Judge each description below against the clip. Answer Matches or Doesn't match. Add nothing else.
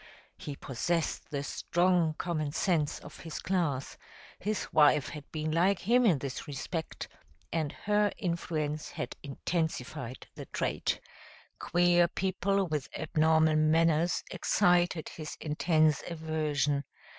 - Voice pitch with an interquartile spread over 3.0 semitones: Doesn't match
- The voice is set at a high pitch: Doesn't match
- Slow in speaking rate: Matches